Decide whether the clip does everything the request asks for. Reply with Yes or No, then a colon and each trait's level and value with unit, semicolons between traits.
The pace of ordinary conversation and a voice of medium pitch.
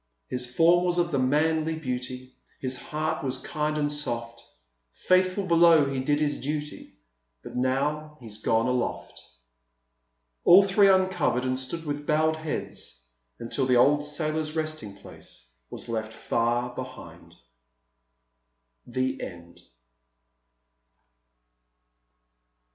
No: slow, 115 wpm; medium, 145 Hz